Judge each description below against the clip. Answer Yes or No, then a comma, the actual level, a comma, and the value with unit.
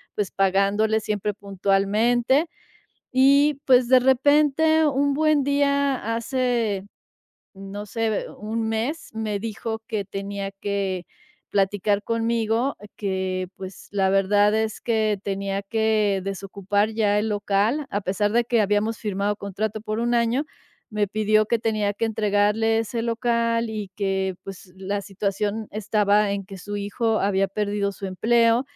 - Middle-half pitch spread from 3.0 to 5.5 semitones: No, narrow, 2.6 semitones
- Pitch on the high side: Yes, high, 210 Hz